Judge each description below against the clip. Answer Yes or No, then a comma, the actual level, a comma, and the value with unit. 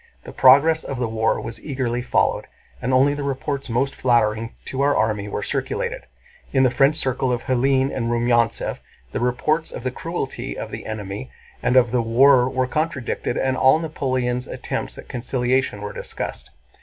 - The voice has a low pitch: Yes, low, 130 Hz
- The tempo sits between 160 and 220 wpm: Yes, average, 175 wpm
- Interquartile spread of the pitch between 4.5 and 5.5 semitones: No, narrow, 2.5 semitones